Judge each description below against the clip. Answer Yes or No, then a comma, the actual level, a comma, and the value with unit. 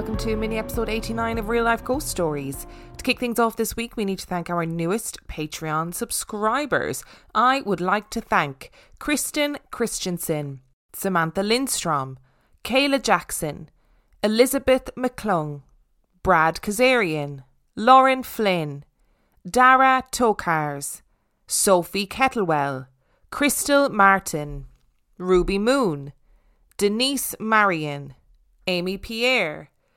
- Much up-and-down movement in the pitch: Yes, wide, 7.4 semitones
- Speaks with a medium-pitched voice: No, high, 195 Hz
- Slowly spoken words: Yes, slow, 105 wpm